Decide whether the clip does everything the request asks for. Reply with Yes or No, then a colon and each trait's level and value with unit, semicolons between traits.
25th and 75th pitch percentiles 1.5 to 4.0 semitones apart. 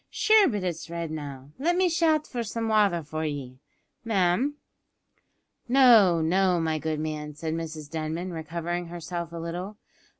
No: average, 5.3 semitones